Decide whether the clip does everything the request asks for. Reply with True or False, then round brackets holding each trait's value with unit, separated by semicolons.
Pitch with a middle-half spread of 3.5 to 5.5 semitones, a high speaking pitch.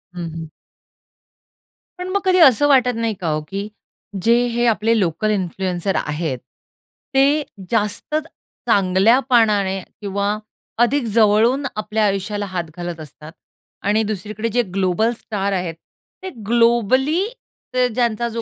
True (4.1 semitones; 215 Hz)